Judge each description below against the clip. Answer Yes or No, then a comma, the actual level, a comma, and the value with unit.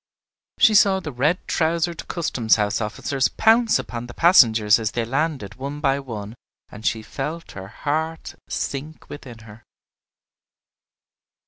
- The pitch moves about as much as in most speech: No, wide, 6.3 semitones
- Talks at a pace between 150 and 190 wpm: No, slow, 135 wpm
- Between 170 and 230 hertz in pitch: No, low, 135 Hz